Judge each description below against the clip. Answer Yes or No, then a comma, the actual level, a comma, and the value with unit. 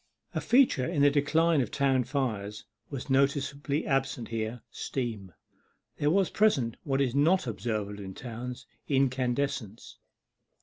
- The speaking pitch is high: No, low, 135 Hz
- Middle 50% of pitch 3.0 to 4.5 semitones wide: Yes, average, 3.6 semitones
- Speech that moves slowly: Yes, slow, 130 wpm